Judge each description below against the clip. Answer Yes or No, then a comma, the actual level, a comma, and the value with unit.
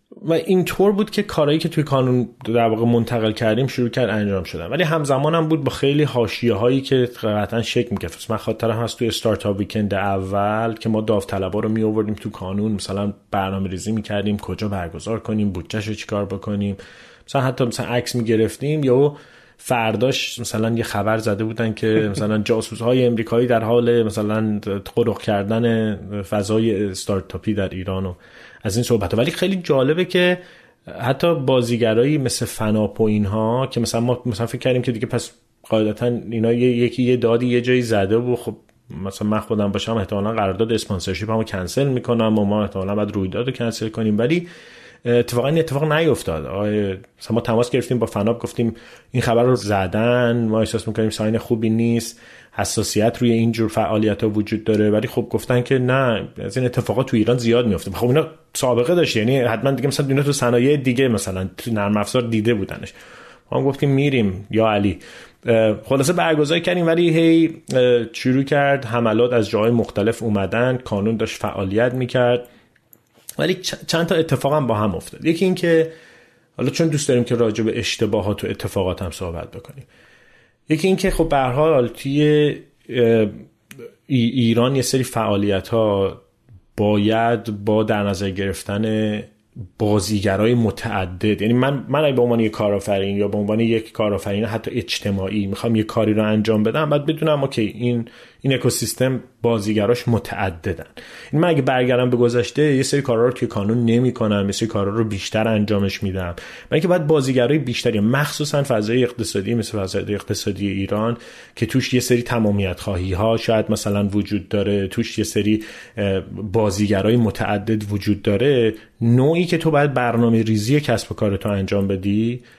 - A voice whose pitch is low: Yes, low, 115 Hz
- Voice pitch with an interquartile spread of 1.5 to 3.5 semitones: Yes, average, 3.1 semitones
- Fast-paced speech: Yes, fast, 170 wpm